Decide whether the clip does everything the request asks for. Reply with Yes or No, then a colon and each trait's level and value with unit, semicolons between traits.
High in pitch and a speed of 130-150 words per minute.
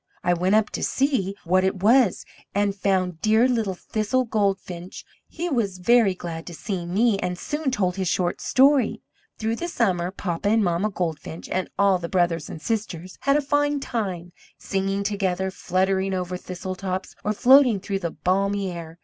No: high, 195 Hz; average, 175 wpm